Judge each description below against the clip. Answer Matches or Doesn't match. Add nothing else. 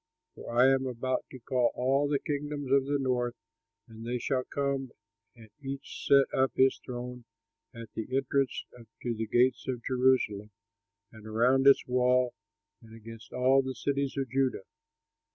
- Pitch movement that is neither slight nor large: Doesn't match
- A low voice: Matches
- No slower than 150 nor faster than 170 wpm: Matches